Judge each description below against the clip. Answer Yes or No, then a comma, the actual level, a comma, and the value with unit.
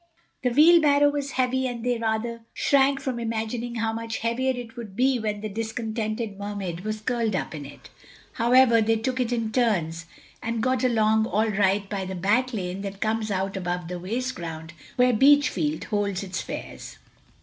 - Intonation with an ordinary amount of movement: Yes, average, 3.8 semitones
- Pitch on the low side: No, high, 225 Hz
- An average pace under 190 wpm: Yes, average, 180 wpm